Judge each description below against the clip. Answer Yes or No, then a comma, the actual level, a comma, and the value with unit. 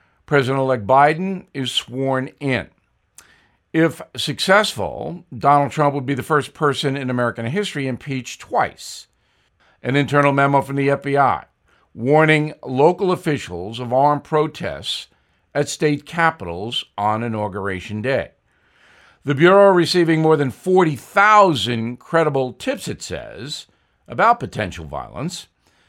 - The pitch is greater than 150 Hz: No, medium, 140 Hz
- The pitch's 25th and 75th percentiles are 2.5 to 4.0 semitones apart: No, average, 4.5 semitones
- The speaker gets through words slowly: Yes, slow, 120 wpm